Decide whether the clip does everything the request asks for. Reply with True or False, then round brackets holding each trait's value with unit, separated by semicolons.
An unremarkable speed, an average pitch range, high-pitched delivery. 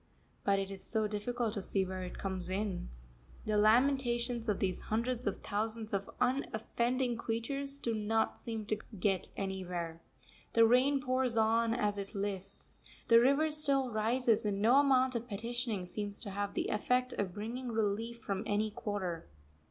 True (165 wpm; 3.4 semitones; 220 Hz)